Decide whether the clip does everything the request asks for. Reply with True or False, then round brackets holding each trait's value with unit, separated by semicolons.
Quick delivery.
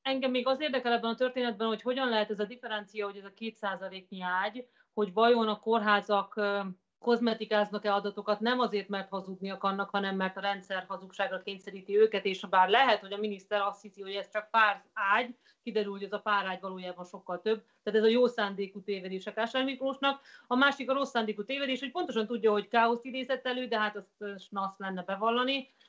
True (195 wpm)